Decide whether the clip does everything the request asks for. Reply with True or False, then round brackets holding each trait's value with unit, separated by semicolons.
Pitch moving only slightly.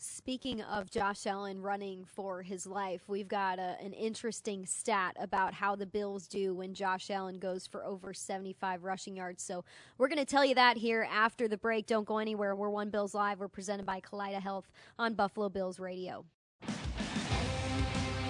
True (2.0 semitones)